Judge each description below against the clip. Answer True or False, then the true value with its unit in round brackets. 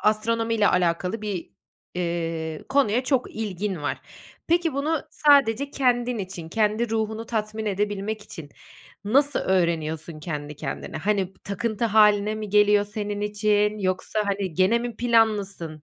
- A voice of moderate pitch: False (210 Hz)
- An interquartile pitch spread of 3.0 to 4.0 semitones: True (3.3 semitones)